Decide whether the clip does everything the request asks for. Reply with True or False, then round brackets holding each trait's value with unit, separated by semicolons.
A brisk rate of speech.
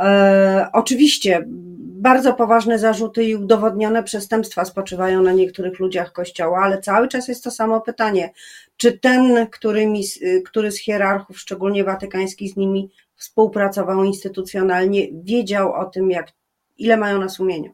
False (130 wpm)